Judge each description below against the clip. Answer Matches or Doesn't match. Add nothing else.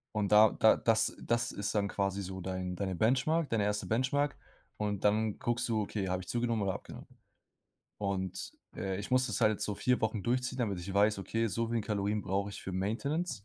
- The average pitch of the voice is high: Doesn't match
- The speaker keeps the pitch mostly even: Doesn't match